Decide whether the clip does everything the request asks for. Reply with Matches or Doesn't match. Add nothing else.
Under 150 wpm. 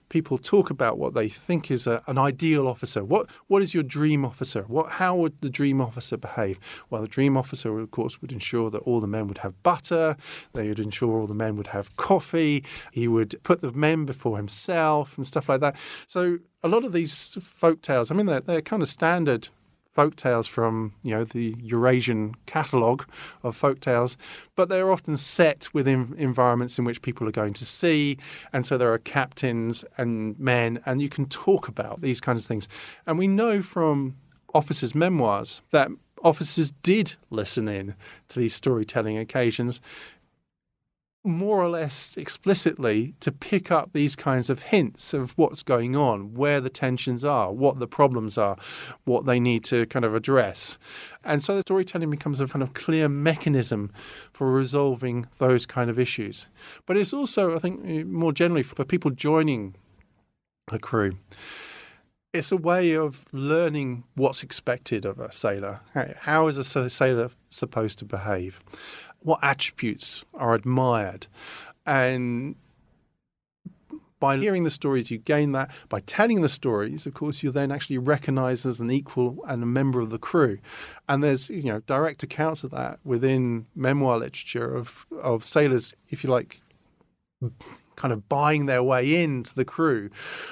Doesn't match